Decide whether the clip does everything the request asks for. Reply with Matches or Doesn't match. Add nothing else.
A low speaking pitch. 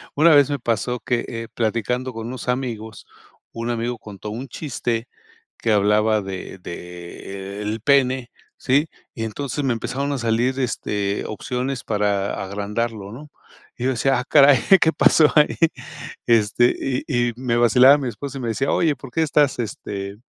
Matches